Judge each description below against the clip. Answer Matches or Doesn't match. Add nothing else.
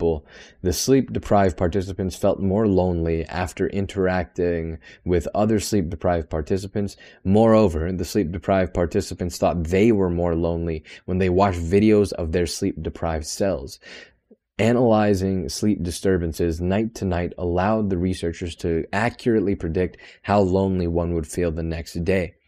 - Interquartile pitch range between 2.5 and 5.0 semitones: Matches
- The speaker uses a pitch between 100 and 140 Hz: Doesn't match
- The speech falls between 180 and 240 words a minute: Doesn't match